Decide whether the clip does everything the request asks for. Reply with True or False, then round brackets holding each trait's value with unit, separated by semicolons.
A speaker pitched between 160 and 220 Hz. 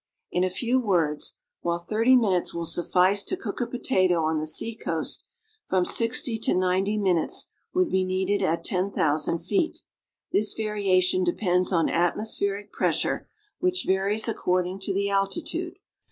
True (190 Hz)